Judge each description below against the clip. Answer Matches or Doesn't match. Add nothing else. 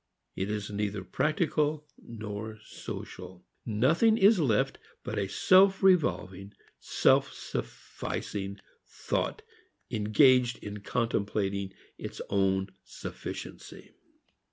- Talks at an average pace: Doesn't match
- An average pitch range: Doesn't match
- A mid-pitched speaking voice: Doesn't match